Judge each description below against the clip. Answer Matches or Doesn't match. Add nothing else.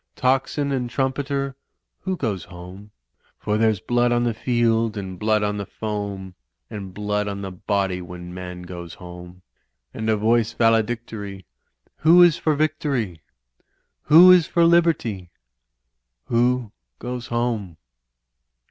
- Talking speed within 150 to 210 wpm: Doesn't match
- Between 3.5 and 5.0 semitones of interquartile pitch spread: Matches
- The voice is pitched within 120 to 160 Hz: Doesn't match